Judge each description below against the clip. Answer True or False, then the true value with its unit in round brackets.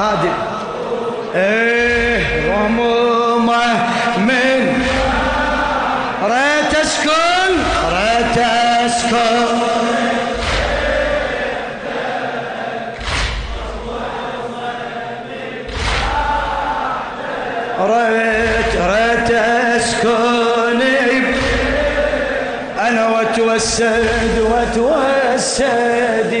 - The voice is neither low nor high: False (235 Hz)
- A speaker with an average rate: False (30 wpm)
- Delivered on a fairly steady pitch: True (2.0 semitones)